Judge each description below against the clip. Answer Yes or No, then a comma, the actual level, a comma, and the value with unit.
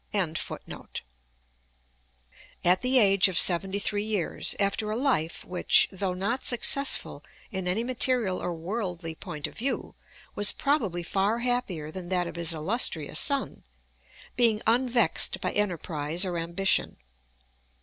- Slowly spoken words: Yes, slow, 130 wpm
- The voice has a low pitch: No, high, 195 Hz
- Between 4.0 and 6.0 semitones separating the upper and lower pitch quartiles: Yes, average, 5.0 semitones